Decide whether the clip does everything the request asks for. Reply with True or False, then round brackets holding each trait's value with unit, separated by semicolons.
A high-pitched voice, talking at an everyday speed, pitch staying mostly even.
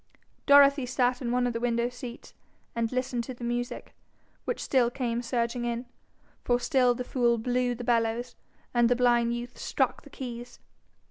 True (245 Hz; 175 wpm; 0.9 semitones)